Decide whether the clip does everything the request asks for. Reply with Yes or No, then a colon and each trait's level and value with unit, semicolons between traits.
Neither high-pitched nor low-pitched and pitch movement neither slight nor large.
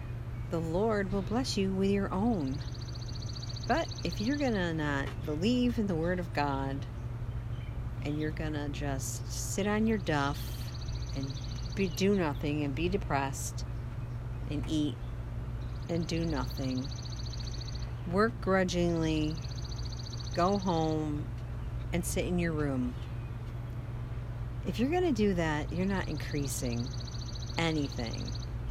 No: low, 125 Hz; average, 4.7 semitones